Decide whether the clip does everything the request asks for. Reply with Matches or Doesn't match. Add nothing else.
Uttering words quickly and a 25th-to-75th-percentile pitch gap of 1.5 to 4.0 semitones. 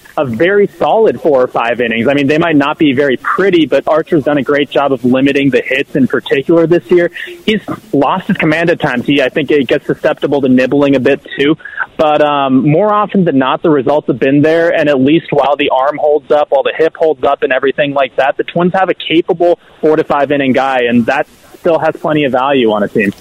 Matches